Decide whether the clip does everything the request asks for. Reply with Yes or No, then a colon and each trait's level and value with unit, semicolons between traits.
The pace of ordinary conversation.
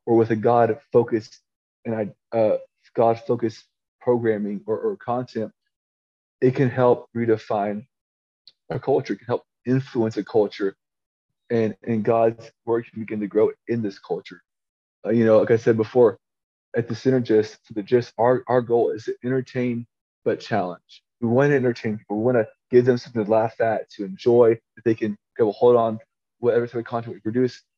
Yes: average, 180 wpm